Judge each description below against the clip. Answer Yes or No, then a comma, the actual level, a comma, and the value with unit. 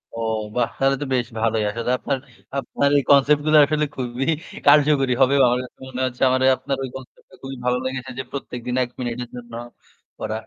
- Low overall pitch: Yes, low, 130 Hz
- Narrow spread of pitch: Yes, narrow, 2.0 semitones